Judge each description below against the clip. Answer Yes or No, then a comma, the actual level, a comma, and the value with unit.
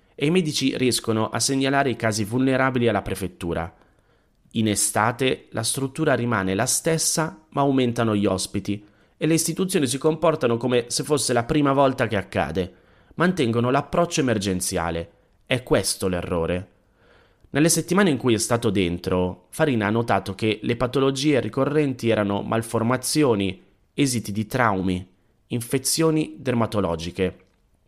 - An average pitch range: No, wide, 5.8 semitones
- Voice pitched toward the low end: Yes, low, 115 Hz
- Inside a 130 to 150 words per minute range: Yes, average, 135 wpm